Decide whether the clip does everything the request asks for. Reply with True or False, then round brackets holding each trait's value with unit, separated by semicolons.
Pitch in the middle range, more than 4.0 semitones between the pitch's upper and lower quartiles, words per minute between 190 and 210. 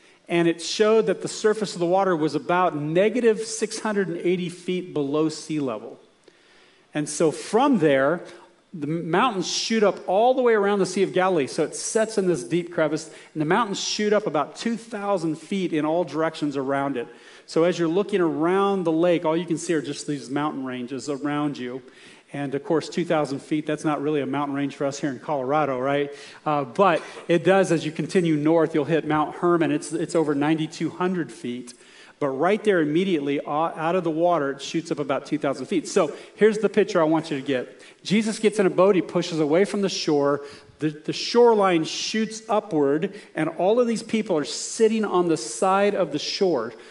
True (165 Hz; 4.5 semitones; 200 wpm)